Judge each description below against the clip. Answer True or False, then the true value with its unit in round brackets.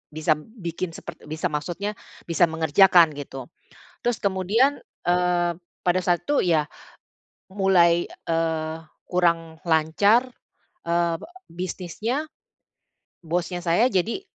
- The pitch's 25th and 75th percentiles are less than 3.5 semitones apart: True (2.7 semitones)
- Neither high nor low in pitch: True (175 Hz)